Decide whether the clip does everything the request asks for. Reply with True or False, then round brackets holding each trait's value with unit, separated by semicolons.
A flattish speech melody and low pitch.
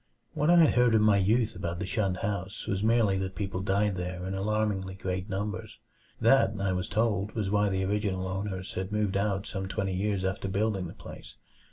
True (2.0 semitones; 100 Hz)